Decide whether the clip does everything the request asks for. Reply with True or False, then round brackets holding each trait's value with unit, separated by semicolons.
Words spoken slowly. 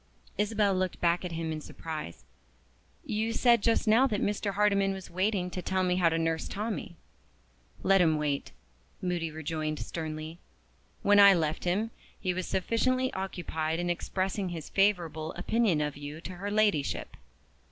False (160 wpm)